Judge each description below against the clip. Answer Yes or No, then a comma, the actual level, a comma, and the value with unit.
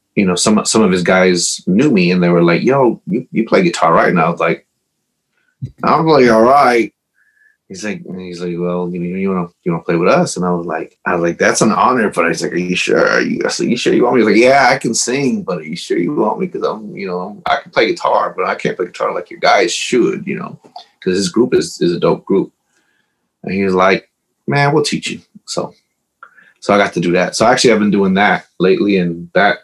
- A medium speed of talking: No, fast, 265 wpm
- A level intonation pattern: Yes, narrow, 1.9 semitones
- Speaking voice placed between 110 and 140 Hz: No, very low, 90 Hz